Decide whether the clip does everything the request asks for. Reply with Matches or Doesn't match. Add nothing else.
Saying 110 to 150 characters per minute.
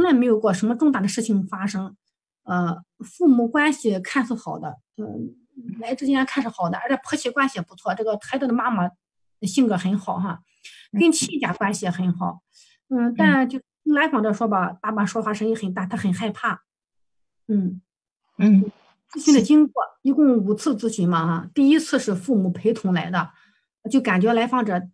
Doesn't match